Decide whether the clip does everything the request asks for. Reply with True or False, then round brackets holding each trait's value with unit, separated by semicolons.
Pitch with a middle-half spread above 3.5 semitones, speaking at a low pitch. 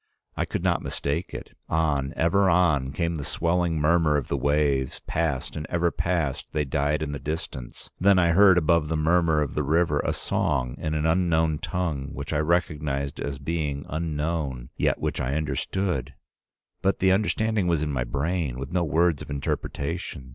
False (3.2 semitones; 80 Hz)